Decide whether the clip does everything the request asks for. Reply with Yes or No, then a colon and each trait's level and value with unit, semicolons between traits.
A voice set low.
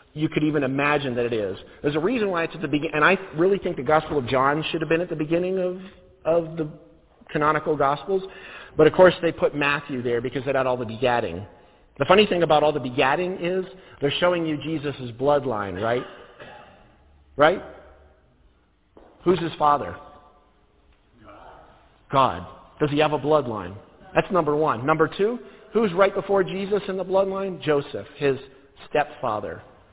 No: medium, 155 Hz